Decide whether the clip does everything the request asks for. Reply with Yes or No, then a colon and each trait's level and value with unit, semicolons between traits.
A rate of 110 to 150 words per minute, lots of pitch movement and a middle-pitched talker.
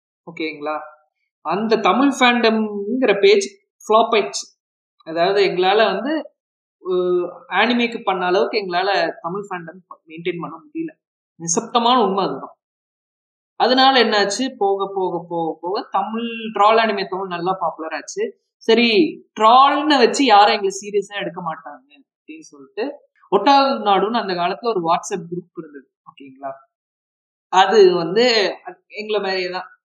No: average, 120 wpm; wide, 6.2 semitones; high, 205 Hz